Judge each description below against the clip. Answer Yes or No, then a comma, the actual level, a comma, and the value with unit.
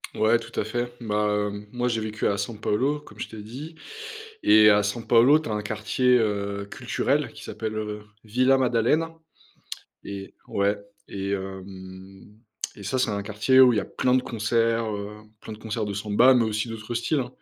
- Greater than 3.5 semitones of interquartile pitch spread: No, average, 2.9 semitones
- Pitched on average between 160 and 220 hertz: No, low, 110 Hz